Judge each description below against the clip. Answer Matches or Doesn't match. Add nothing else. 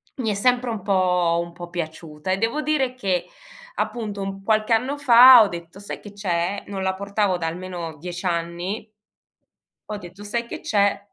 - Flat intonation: Doesn't match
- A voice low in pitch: Doesn't match